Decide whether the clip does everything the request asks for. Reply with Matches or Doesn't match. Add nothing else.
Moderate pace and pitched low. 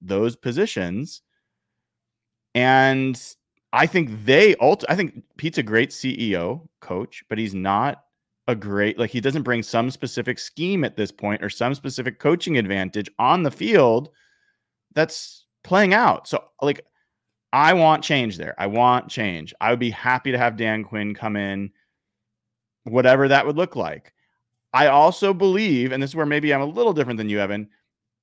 Matches